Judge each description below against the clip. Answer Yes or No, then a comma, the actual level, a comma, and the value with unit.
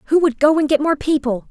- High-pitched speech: Yes, very high, 295 Hz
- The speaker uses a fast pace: Yes, fast, 280 wpm